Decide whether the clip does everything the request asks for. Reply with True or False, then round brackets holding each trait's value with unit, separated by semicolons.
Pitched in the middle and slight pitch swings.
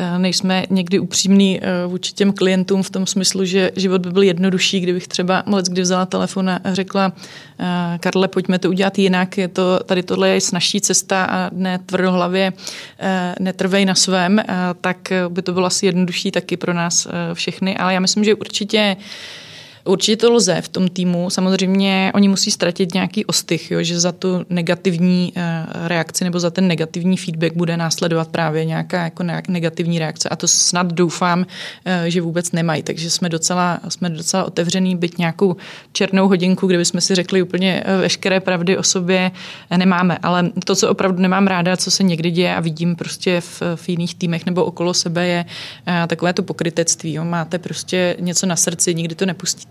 True (180 Hz; 1.5 semitones)